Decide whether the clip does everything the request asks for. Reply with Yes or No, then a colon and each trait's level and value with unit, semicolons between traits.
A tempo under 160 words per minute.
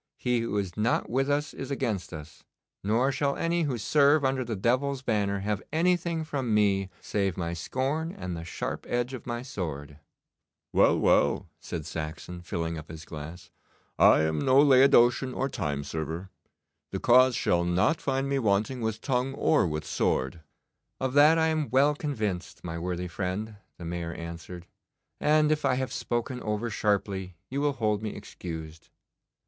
No: average, 170 wpm